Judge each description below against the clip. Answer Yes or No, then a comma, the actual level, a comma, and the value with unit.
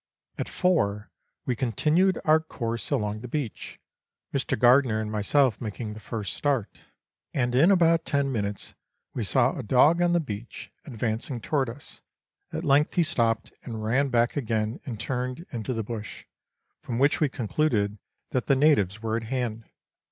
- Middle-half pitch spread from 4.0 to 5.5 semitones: Yes, average, 4.6 semitones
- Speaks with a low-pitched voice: Yes, low, 125 Hz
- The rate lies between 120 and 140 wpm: No, average, 165 wpm